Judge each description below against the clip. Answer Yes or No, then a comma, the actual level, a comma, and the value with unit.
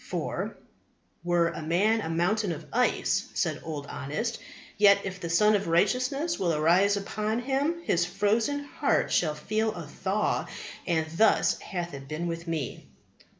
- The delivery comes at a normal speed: Yes, average, 155 wpm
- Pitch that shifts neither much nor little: Yes, average, 4.6 semitones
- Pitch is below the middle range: No, high, 190 Hz